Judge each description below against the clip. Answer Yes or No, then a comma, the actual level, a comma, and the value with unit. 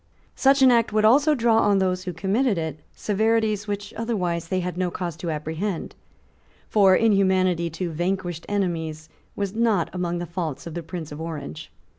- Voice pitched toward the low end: No, medium, 185 Hz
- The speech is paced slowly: No, average, 175 wpm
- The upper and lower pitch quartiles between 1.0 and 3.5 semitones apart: No, average, 3.9 semitones